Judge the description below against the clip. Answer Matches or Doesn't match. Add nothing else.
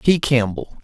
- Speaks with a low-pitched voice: Matches